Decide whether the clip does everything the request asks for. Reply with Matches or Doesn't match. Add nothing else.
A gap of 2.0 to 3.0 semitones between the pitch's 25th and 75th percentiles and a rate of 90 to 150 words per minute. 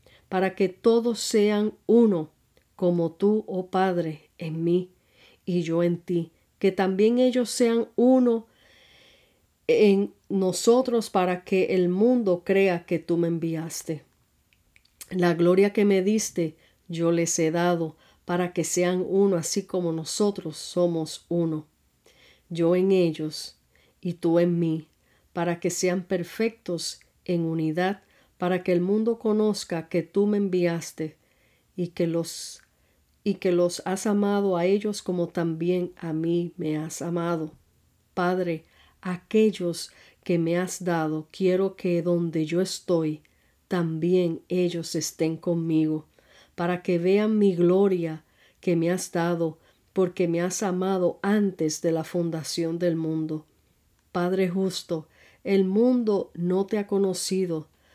Matches